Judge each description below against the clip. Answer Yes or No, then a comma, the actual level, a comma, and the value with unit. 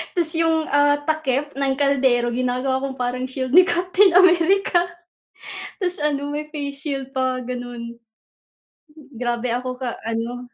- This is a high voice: Yes, very high, 270 Hz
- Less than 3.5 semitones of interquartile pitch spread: No, average, 3.9 semitones